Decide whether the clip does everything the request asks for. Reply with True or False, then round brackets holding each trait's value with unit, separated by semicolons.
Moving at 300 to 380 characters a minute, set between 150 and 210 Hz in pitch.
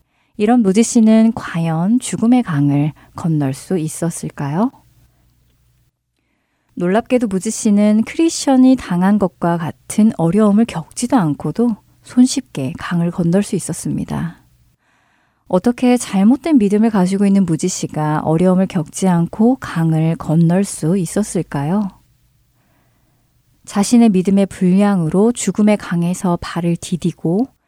False (260 characters per minute; 190 Hz)